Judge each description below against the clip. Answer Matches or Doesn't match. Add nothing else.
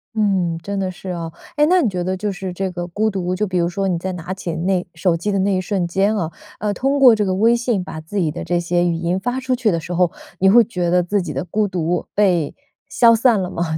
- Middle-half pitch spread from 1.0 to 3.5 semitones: Matches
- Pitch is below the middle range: Doesn't match